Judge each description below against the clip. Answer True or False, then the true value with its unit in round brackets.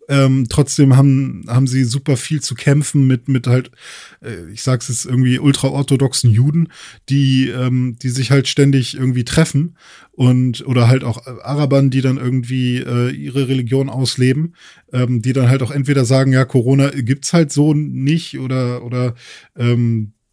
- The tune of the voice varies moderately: False (1.8 semitones)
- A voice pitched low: True (130 Hz)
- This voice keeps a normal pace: True (160 wpm)